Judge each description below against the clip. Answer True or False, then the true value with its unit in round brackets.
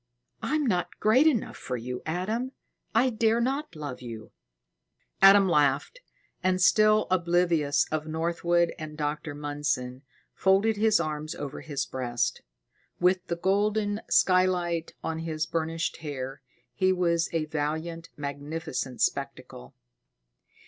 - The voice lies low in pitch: False (170 Hz)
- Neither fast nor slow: False (125 wpm)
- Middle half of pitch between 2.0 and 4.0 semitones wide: False (4.5 semitones)